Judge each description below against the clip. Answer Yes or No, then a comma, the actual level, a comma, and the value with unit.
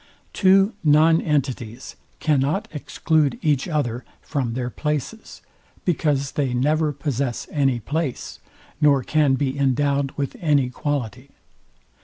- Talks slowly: Yes, slow, 115 wpm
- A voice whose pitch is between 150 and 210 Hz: No, medium, 140 Hz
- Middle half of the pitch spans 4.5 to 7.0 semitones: No, average, 2.7 semitones